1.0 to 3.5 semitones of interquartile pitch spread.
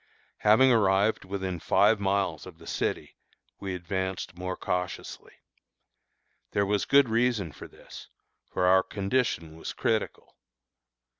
Yes: average, 2.9 semitones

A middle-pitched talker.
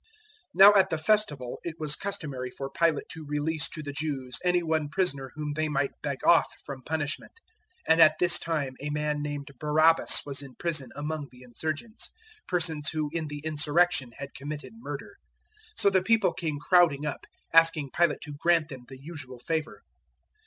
Yes: medium, 150 Hz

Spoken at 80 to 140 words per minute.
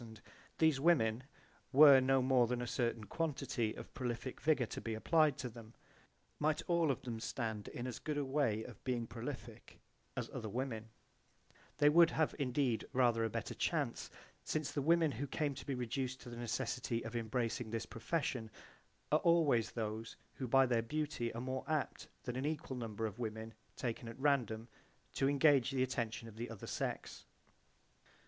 No: average, 175 wpm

